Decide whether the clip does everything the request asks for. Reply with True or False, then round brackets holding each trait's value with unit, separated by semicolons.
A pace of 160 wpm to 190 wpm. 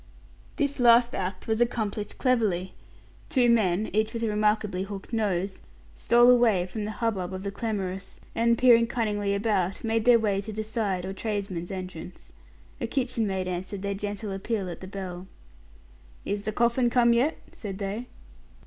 True (165 wpm)